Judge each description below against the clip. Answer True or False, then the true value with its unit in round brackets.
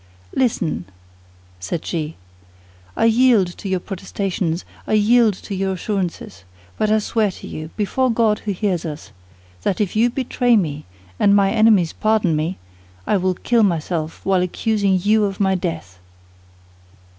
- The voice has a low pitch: False (195 Hz)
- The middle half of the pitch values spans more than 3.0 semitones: True (3.9 semitones)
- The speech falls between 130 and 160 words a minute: True (150 wpm)